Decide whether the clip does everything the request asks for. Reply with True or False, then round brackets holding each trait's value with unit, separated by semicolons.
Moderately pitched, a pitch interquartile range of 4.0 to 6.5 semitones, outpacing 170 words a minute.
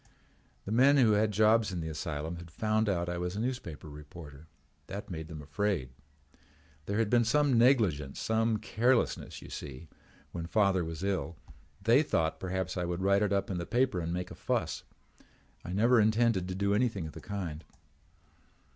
False (95 Hz; 4.7 semitones; 180 wpm)